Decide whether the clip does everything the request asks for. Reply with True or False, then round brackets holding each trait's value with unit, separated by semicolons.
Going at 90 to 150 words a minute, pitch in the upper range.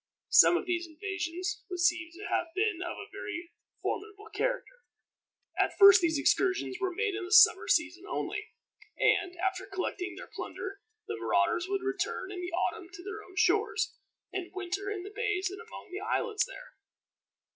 False (175 wpm; 385 Hz)